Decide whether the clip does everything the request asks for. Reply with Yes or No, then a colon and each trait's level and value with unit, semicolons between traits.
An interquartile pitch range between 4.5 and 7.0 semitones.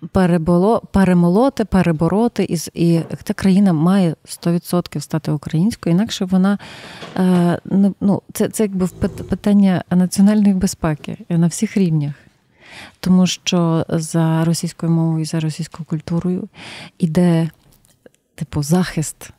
No: average, 3.0 semitones